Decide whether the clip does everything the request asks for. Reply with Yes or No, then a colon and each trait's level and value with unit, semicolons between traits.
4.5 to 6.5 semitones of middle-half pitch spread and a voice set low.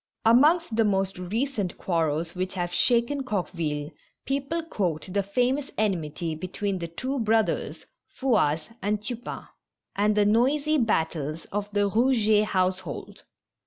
No: wide, 5.4 semitones; high, 205 Hz